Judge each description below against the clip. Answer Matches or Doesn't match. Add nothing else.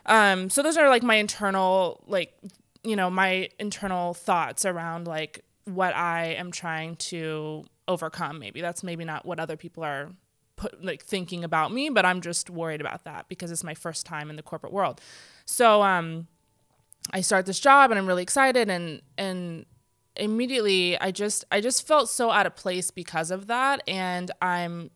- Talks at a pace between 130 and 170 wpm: Doesn't match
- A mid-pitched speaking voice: Matches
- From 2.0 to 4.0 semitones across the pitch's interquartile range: Matches